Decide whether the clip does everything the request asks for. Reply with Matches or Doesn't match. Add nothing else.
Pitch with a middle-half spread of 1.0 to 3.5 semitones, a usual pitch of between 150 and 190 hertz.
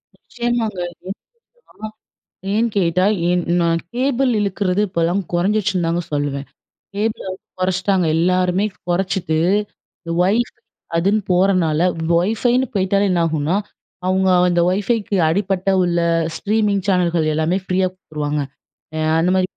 Matches